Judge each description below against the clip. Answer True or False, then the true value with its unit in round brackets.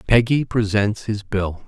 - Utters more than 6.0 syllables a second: False (4.1 syllables/s)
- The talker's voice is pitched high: False (105 Hz)